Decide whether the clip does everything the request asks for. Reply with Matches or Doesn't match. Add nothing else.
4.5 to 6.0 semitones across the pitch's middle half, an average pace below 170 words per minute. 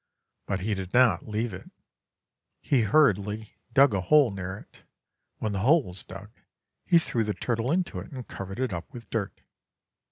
Doesn't match